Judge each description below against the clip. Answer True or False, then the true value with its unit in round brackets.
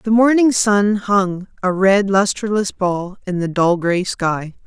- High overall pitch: True (195 Hz)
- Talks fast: False (165 wpm)